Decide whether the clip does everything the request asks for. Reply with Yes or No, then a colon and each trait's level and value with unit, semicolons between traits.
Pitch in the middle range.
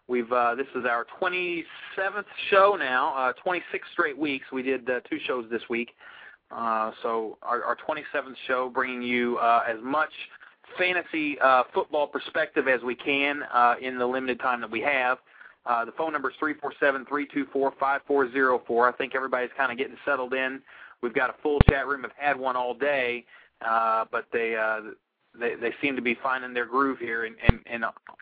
No: low, 130 Hz